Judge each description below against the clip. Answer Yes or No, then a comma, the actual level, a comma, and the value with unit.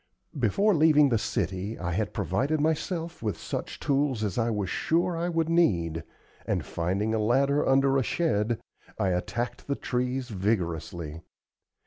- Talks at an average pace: Yes, average, 150 wpm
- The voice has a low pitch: Yes, low, 120 Hz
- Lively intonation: Yes, wide, 7.2 semitones